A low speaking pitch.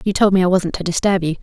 No: medium, 185 Hz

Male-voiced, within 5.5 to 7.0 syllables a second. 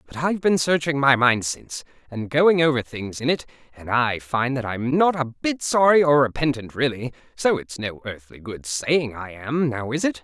No: male; 4.9 syllables/s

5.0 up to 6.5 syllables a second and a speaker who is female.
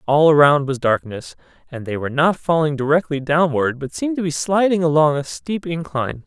No: 5.5 syllables/s; male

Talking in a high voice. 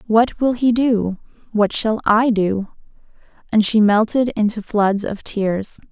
Yes: high, 215 Hz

